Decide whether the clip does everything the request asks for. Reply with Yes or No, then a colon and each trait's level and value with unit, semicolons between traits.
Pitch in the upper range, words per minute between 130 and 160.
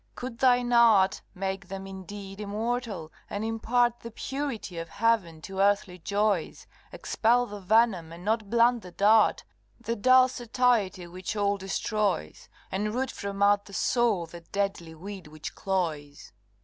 Yes: high, 205 Hz; average, 150 wpm